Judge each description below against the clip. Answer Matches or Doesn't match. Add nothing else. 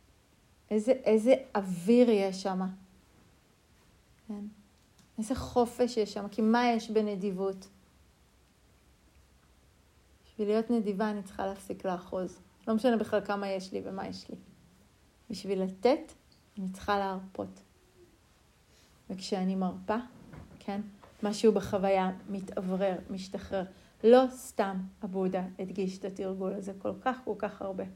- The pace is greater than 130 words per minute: Doesn't match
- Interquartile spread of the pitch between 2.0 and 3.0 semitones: Matches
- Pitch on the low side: Doesn't match